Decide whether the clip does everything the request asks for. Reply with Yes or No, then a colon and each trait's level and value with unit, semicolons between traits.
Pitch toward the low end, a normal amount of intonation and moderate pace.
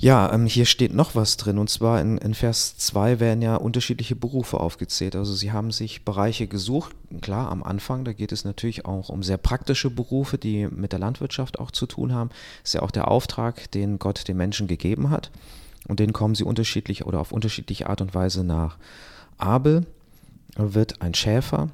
No: low, 110 Hz; average, 3.5 semitones; fast, 200 wpm